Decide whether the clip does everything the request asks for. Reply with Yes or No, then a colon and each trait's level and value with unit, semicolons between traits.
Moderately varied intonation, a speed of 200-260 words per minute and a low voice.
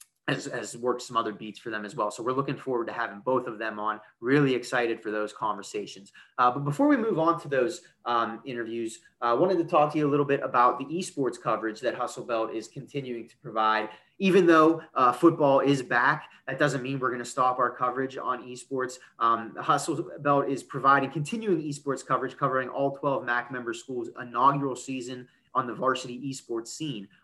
Yes: average, 3.4 semitones; fast, 205 wpm; low, 130 Hz